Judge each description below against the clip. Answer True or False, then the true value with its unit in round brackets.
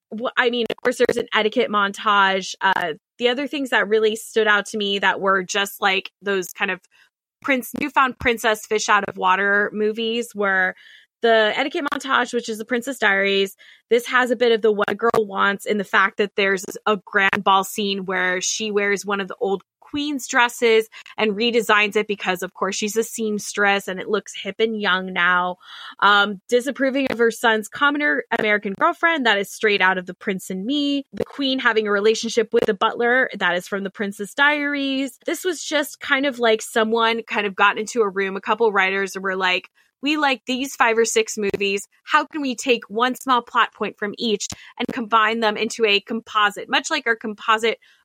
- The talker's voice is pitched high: True (220 Hz)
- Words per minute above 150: True (200 wpm)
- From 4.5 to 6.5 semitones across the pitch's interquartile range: False (3.3 semitones)